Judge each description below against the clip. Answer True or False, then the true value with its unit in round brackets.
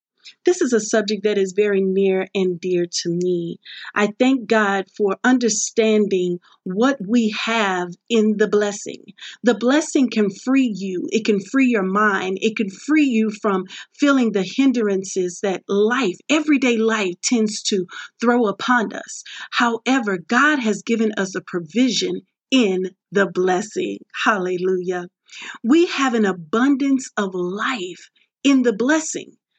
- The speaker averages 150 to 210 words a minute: False (140 wpm)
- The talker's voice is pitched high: True (215 Hz)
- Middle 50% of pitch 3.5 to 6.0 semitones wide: True (4.4 semitones)